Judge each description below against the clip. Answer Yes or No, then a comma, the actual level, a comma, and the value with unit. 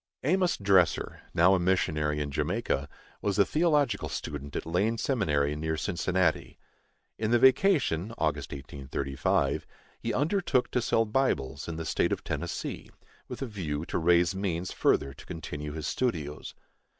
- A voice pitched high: No, very low, 90 Hz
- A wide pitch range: Yes, wide, 7.3 semitones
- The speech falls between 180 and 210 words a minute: No, average, 150 wpm